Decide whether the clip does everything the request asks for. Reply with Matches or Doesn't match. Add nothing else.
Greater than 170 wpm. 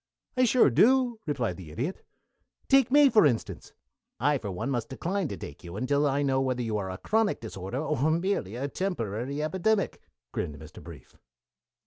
Matches